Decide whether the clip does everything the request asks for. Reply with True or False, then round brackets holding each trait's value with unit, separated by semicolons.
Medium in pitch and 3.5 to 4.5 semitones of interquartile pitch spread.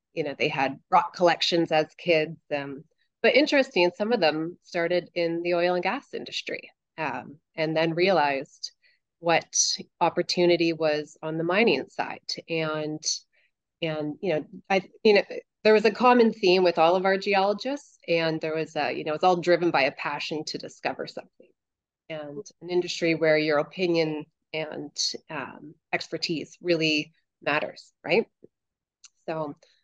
False (170 Hz; 3.1 semitones)